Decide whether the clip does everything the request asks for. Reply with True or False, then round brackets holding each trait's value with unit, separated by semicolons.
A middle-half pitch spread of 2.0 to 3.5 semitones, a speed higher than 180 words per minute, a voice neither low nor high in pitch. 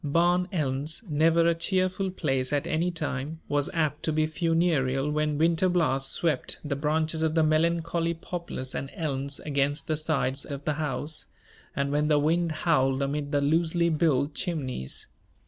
False (2.9 semitones; 165 wpm; 155 Hz)